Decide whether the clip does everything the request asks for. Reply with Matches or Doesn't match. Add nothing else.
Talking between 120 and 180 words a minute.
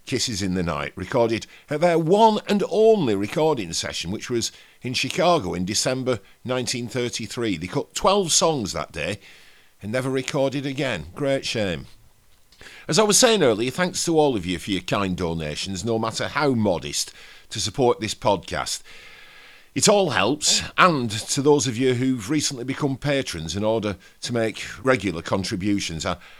Matches